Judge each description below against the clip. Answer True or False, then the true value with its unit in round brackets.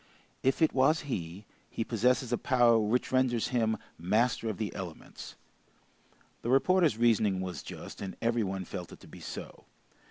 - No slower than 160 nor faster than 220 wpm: True (165 wpm)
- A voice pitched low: True (115 Hz)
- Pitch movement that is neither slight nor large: True (4.0 semitones)